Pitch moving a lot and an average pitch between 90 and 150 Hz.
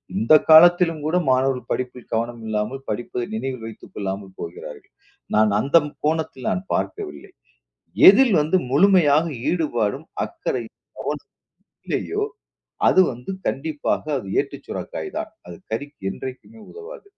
Yes: wide, 6.3 semitones; low, 135 Hz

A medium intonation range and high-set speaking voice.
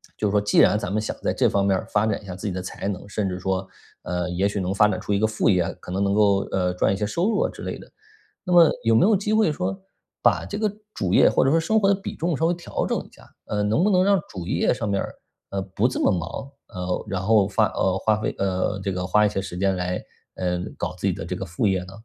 No: average, 3.4 semitones; low, 100 Hz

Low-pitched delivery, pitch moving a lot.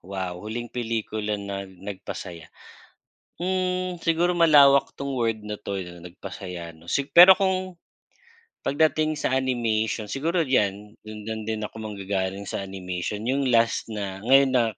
Yes: low, 110 Hz; wide, 5.9 semitones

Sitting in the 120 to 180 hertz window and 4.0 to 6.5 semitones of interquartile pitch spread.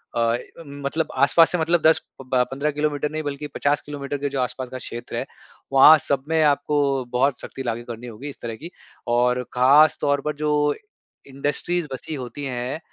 No: medium, 140 Hz; average, 3.0 semitones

